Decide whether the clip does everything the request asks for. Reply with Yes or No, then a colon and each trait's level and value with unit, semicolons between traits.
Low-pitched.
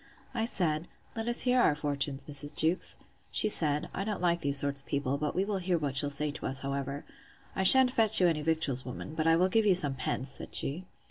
No: medium, 155 Hz